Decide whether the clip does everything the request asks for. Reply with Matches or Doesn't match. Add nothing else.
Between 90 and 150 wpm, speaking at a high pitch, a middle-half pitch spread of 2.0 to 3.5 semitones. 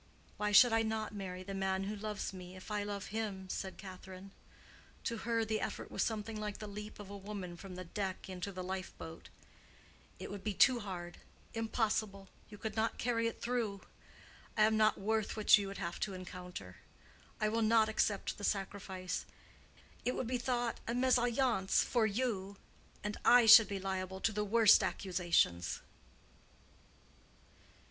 Doesn't match